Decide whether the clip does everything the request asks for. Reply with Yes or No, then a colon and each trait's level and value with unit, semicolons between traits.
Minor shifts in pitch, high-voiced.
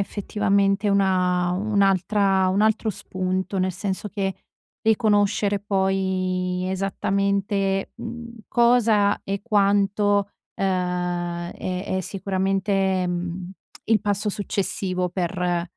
Yes: narrow, 1.7 semitones; high, 195 Hz